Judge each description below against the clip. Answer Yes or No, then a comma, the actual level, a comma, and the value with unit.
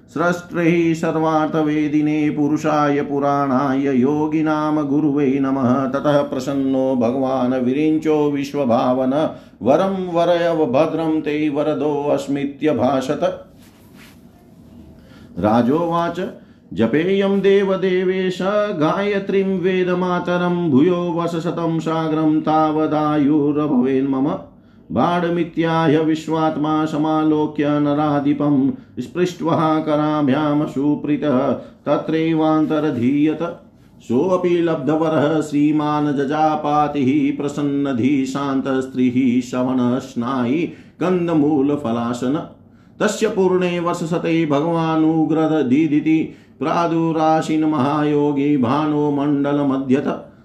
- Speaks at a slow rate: Yes, slow, 55 wpm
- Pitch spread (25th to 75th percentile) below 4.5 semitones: Yes, average, 2.7 semitones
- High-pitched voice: No, medium, 150 Hz